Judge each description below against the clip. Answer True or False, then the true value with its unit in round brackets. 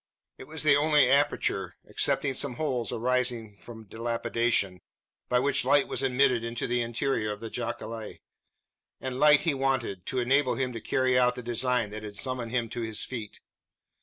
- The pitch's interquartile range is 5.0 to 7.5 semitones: False (2.7 semitones)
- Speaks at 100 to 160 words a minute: False (175 wpm)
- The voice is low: True (125 Hz)